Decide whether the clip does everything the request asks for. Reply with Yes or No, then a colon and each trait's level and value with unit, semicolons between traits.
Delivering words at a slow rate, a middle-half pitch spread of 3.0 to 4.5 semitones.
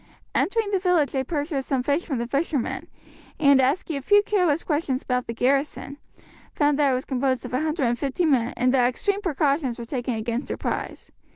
No: average, 185 wpm; average, 3.6 semitones